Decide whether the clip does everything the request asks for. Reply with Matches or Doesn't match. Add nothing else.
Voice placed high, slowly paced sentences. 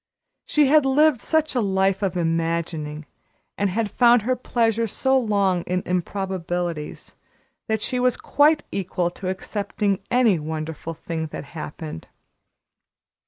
Matches